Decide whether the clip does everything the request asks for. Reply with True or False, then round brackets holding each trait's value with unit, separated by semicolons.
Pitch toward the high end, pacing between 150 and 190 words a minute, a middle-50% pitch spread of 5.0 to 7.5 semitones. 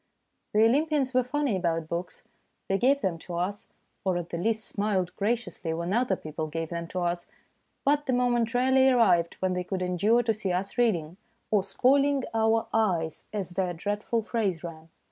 True (200 Hz; 185 wpm; 5.5 semitones)